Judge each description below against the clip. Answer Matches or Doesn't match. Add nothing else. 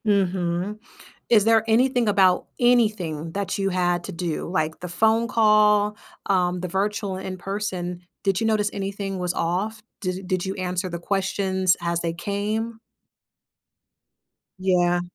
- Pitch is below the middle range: Doesn't match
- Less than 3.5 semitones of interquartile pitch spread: Matches